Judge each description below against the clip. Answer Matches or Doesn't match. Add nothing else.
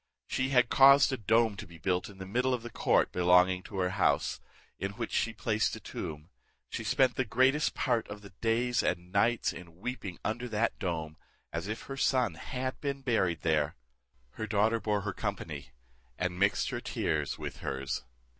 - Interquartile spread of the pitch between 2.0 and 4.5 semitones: Doesn't match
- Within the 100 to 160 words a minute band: Doesn't match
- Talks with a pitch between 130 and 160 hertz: Doesn't match